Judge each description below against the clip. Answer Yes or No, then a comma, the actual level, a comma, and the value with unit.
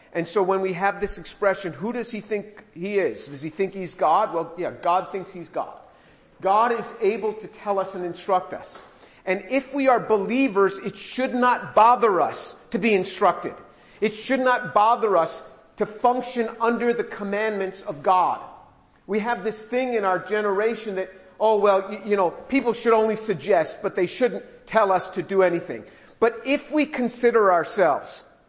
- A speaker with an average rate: Yes, average, 185 wpm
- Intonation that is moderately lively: Yes, average, 3.5 semitones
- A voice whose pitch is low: No, high, 210 Hz